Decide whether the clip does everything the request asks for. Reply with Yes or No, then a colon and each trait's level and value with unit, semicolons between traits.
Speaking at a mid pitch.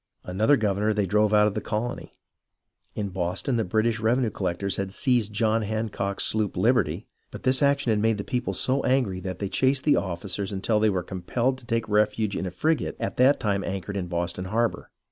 No: low, 105 Hz